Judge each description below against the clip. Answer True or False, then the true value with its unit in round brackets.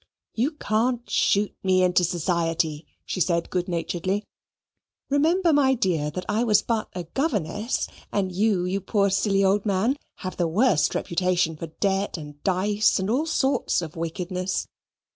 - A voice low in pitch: False (190 Hz)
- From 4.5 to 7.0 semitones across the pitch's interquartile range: False (3.7 semitones)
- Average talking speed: True (155 wpm)